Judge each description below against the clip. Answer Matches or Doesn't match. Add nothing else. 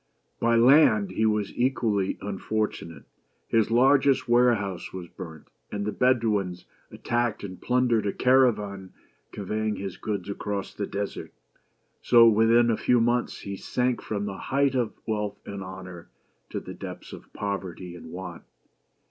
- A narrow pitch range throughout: Doesn't match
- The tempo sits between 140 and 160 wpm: Matches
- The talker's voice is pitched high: Doesn't match